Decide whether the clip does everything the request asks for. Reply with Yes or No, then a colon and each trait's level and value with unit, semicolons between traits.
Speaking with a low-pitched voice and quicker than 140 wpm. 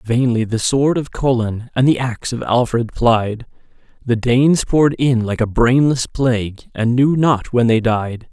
Yes: low, 120 Hz; average, 180 wpm